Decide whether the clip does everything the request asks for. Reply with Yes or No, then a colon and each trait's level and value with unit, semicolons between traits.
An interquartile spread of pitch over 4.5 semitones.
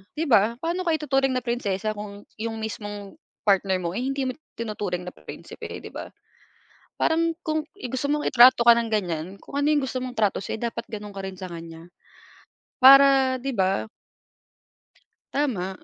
Yes: wide, 5.4 semitones